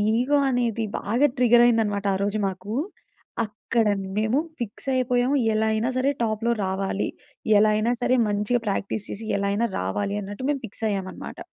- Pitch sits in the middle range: No, high, 220 Hz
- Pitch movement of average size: Yes, average, 3.2 semitones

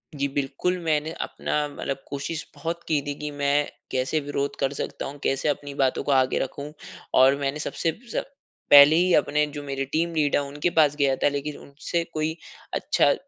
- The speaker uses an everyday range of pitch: No, narrow, 1.6 semitones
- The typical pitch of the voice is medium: Yes, medium, 145 Hz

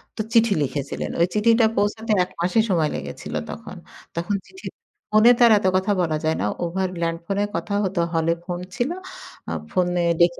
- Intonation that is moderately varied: Yes, average, 4.1 semitones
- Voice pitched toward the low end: No, medium, 185 Hz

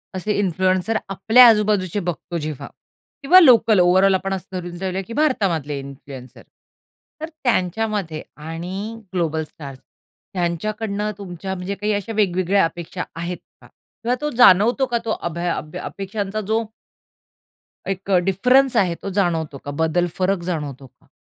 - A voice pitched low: No, high, 190 Hz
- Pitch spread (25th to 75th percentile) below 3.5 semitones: No, average, 3.8 semitones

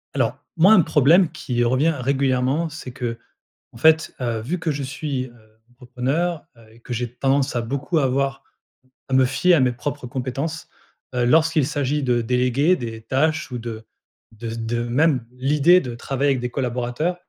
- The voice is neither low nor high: No, low, 130 Hz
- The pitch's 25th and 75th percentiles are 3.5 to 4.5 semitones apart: Yes, average, 3.8 semitones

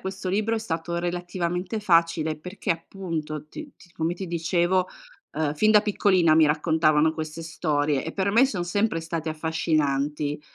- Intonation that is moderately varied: Yes, average, 3.1 semitones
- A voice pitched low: No, medium, 165 Hz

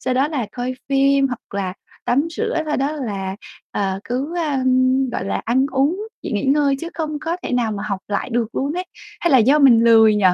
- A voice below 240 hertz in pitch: No, very high, 265 Hz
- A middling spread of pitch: Yes, average, 5.0 semitones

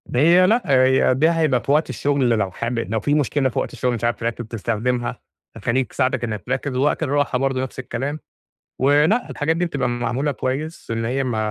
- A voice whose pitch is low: Yes, low, 130 Hz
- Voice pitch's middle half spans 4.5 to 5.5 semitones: No, average, 3.3 semitones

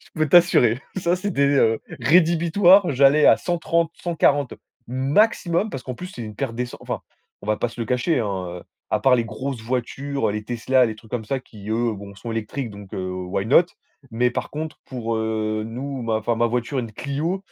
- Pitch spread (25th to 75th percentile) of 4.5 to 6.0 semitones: Yes, wide, 5.4 semitones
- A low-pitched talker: Yes, low, 125 Hz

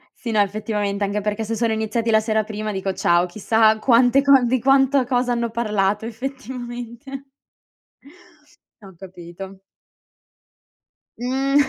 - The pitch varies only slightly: No, average, 3.1 semitones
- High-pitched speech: Yes, high, 225 Hz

